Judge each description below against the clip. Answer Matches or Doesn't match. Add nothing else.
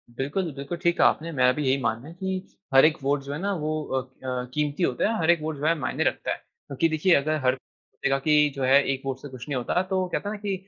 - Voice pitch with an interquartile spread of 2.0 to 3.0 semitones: Doesn't match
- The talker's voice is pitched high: Doesn't match